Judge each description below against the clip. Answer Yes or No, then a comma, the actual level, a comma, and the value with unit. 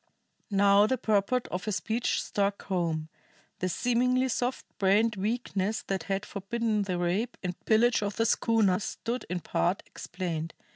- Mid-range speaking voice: No, high, 205 Hz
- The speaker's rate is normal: Yes, average, 150 wpm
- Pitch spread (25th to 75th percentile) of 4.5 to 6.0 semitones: No, average, 3.7 semitones